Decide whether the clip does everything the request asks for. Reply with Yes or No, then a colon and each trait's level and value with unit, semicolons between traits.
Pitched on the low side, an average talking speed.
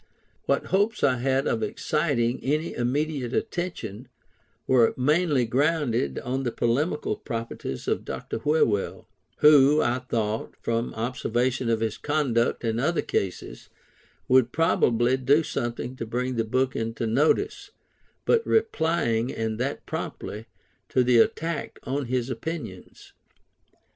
No: low, 125 Hz; slow, 130 wpm